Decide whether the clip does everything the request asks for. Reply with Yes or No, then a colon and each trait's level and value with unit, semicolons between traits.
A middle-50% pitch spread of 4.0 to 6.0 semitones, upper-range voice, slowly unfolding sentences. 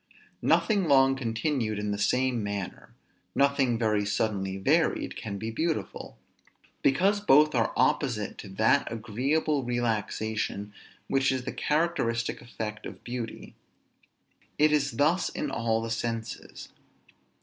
No: average, 4.3 semitones; low, 120 Hz; slow, 125 wpm